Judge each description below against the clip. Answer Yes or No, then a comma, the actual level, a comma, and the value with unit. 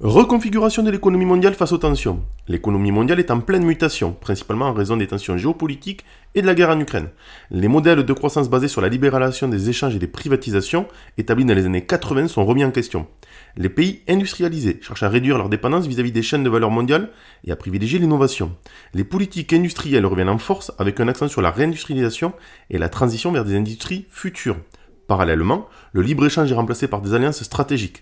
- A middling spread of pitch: No, wide, 7.8 semitones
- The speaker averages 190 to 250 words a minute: Yes, average, 200 wpm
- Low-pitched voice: Yes, low, 130 Hz